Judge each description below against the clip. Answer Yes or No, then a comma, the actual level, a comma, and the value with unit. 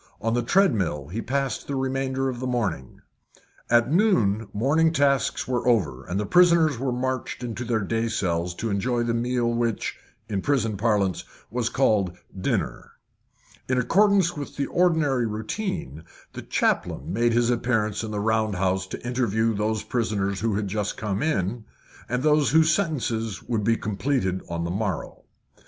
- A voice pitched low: Yes, low, 115 Hz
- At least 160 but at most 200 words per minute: Yes, average, 165 wpm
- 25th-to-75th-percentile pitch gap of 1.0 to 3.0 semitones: No, average, 4.4 semitones